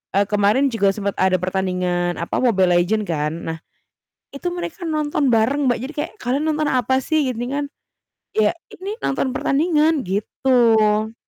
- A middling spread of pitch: No, wide, 6.5 semitones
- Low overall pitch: No, high, 230 Hz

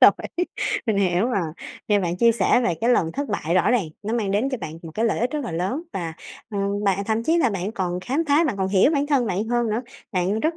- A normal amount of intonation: Yes, average, 4.9 semitones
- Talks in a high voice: Yes, high, 215 Hz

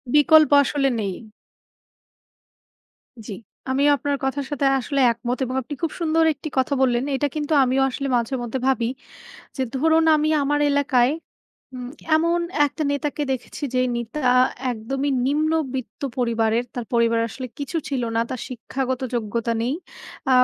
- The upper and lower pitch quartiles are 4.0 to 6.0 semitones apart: No, average, 3.3 semitones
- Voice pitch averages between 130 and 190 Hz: No, very high, 265 Hz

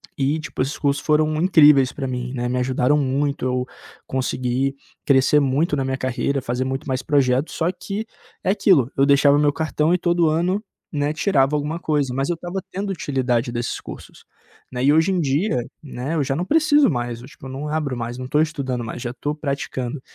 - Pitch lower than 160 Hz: Yes, medium, 140 Hz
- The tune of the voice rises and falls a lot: No, average, 3.4 semitones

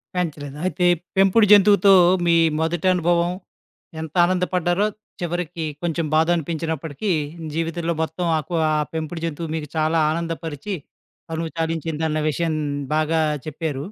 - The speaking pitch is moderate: Yes, medium, 165 Hz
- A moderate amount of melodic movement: No, narrow, 1.7 semitones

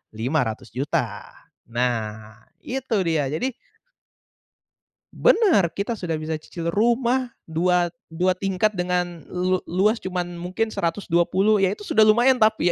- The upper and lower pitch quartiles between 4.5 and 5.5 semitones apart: Yes, average, 5.0 semitones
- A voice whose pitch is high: No, medium, 180 Hz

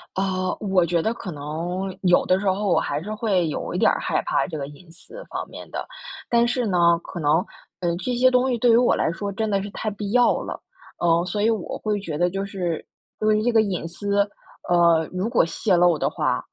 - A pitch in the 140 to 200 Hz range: Yes, high, 190 Hz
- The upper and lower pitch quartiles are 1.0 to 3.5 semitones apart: No, average, 3.9 semitones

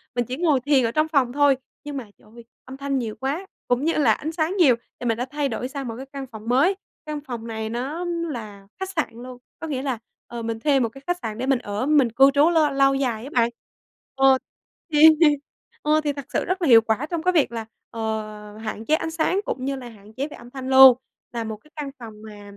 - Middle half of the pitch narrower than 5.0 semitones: Yes, average, 4.3 semitones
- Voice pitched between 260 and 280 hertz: Yes, very high, 265 Hz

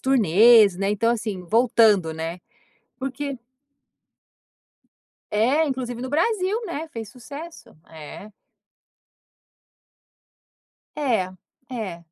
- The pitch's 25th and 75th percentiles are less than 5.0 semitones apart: No, wide, 5.4 semitones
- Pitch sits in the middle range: No, high, 235 Hz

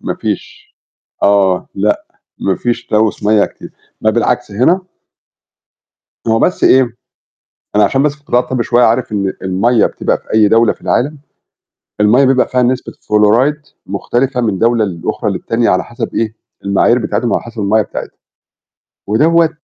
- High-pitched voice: No, low, 115 Hz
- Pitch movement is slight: No, average, 3.3 semitones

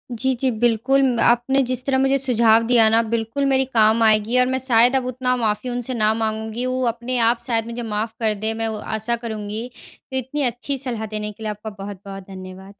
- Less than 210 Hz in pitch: No, high, 230 Hz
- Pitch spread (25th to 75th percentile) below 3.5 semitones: Yes, narrow, 2.6 semitones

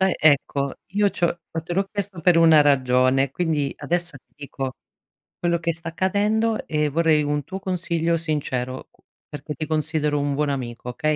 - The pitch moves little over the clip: No, average, 3.5 semitones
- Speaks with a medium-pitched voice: Yes, medium, 155 Hz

